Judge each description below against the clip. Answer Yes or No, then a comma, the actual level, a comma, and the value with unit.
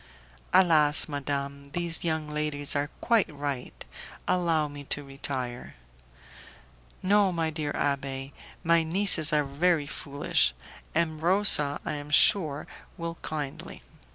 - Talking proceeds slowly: Yes, slow, 120 wpm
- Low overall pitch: No, medium, 150 Hz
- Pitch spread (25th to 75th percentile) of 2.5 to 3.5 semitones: Yes, average, 2.9 semitones